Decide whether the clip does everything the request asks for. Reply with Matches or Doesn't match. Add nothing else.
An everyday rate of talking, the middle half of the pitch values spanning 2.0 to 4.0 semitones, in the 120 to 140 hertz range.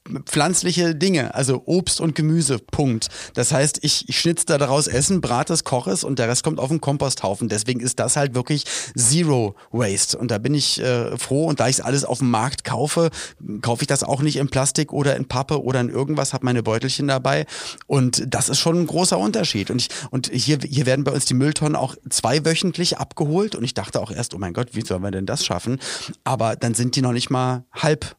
Doesn't match